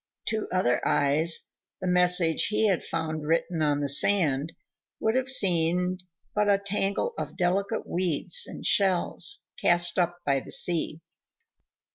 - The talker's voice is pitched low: No, medium, 175 Hz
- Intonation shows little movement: No, average, 3.4 semitones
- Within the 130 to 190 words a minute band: Yes, average, 140 wpm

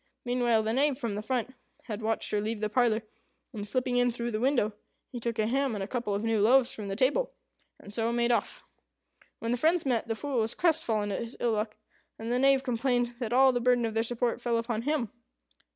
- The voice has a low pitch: No, high, 235 Hz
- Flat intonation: Yes, narrow, 2.3 semitones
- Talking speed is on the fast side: Yes, fast, 230 wpm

